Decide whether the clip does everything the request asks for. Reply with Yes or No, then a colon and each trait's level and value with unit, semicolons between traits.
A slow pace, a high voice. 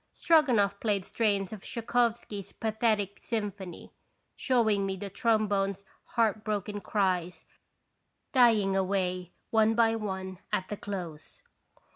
Yes: slow, 115 wpm; high, 205 Hz